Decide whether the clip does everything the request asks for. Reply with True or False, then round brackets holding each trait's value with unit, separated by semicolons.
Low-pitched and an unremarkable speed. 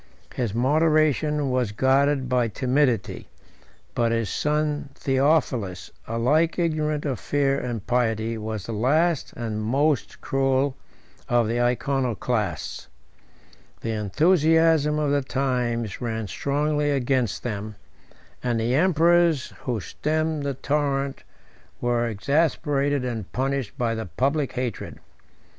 False (130 Hz; 115 wpm)